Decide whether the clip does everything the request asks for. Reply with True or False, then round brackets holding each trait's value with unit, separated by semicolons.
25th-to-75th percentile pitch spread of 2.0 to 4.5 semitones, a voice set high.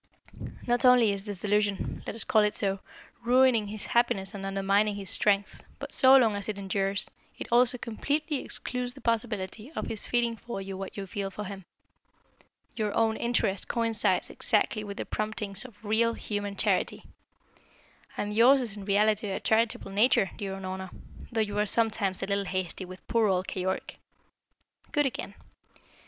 True (2.9 semitones; 210 Hz)